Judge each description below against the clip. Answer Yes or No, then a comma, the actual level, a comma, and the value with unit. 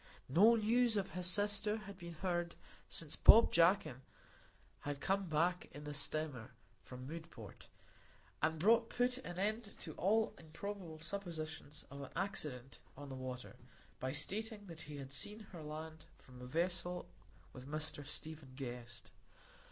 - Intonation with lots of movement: Yes, wide, 5.7 semitones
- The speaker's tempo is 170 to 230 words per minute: No, average, 145 wpm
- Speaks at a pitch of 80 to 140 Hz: No, medium, 165 Hz